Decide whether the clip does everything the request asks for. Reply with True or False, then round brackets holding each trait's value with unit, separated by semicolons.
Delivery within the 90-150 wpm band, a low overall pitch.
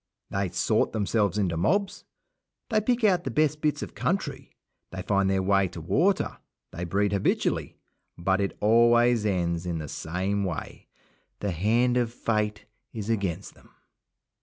False (160 wpm; 100 Hz)